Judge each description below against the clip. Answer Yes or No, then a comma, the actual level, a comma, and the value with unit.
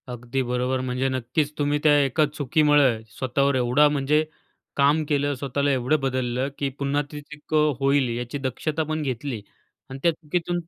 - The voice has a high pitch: No, medium, 140 Hz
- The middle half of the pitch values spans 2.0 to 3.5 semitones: Yes, narrow, 2.5 semitones